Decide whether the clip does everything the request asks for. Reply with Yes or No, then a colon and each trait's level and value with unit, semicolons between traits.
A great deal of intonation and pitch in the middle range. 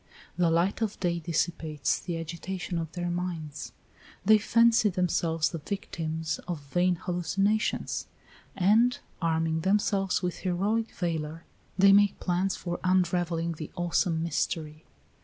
No: average, 2.9 semitones; medium, 175 Hz